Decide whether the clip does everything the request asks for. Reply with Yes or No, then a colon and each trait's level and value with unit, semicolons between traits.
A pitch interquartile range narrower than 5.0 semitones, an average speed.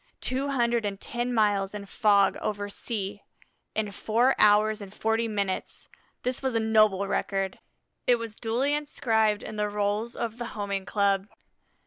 Yes: narrow, 2.6 semitones; average, 155 wpm